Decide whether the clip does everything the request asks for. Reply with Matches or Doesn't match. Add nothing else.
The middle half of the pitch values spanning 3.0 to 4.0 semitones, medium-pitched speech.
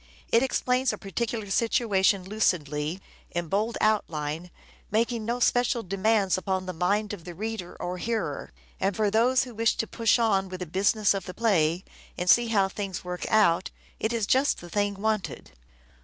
Doesn't match